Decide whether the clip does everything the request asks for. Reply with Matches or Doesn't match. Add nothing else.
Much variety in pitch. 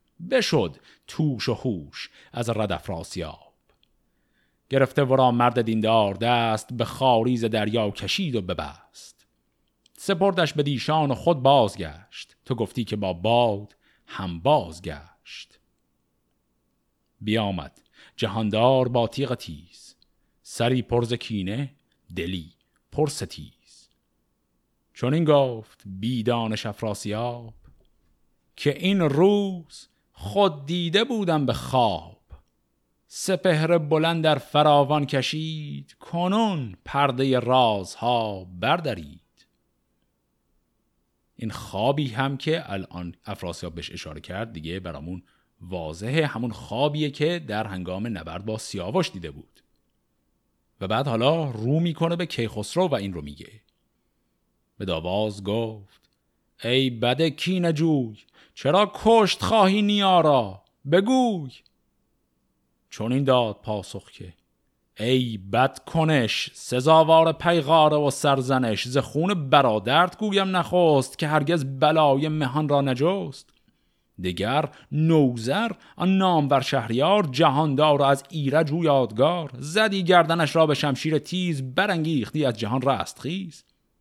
Matches